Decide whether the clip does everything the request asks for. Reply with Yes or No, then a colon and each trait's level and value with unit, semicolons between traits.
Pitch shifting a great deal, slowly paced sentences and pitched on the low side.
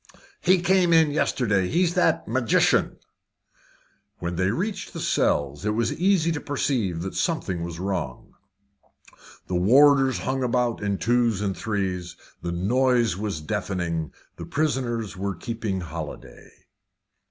Yes: wide, 6.8 semitones; slow, 130 wpm; low, 110 Hz